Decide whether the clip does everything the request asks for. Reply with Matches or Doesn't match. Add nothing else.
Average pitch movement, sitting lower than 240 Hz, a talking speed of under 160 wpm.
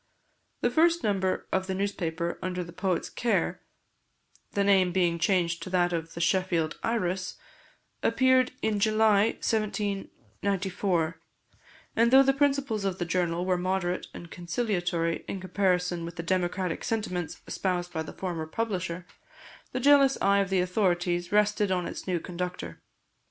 Matches